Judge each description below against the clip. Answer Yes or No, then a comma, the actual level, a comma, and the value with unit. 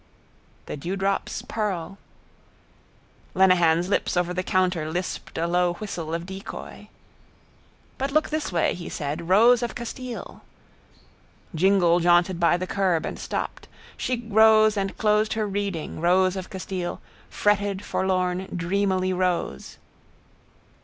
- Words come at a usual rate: No, slow, 125 wpm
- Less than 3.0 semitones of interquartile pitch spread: Yes, narrow, 2.6 semitones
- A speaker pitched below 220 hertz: Yes, medium, 185 Hz